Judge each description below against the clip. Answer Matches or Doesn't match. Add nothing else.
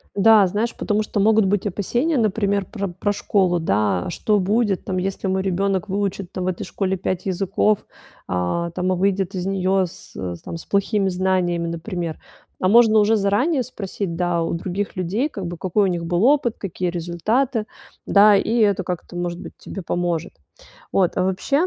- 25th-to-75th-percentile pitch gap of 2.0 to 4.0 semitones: Matches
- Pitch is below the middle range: Doesn't match